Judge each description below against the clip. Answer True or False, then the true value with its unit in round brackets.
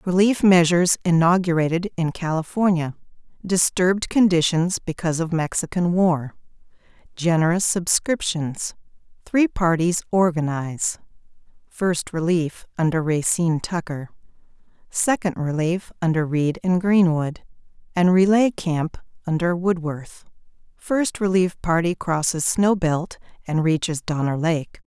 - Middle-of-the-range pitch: True (170 Hz)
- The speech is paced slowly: True (90 wpm)